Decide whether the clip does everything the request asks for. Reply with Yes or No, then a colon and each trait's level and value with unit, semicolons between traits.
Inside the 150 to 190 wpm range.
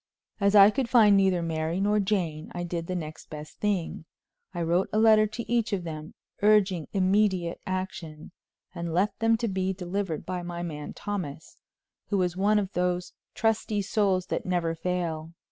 Yes: average, 175 wpm